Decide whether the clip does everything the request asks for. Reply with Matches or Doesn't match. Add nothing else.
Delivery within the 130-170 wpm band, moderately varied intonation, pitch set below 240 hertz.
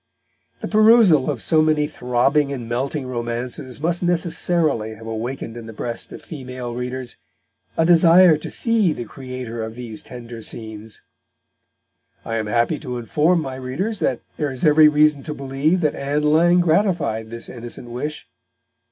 Matches